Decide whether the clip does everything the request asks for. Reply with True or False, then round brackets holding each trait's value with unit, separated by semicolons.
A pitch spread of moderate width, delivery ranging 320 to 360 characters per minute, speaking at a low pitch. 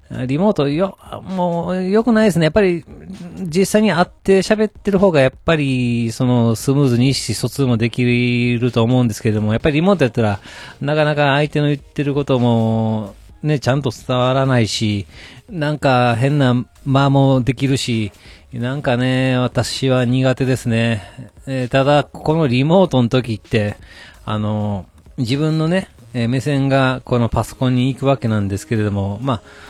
True (4.1 semitones; 325 characters per minute; 130 Hz)